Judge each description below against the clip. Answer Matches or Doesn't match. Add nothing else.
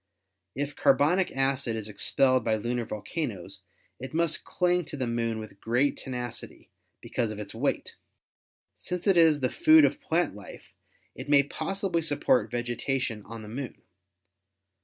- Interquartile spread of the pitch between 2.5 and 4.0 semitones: Doesn't match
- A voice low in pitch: Matches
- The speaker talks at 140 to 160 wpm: Matches